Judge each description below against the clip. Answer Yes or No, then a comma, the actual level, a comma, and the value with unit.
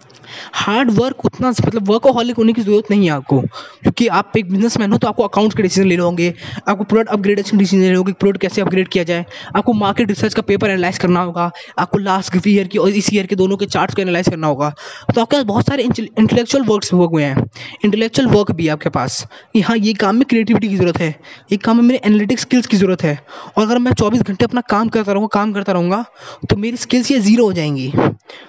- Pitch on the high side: Yes, high, 205 Hz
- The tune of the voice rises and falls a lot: No, average, 4.0 semitones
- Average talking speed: No, fast, 245 wpm